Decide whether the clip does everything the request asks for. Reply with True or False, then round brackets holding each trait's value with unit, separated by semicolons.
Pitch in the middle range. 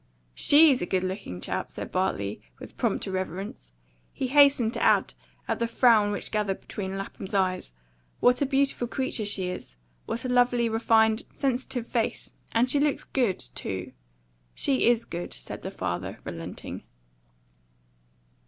False (220 Hz)